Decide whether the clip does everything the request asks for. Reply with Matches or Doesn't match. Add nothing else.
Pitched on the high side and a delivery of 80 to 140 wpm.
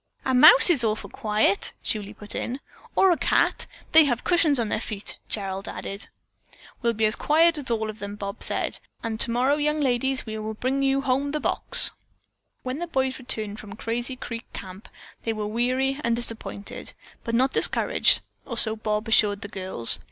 Doesn't match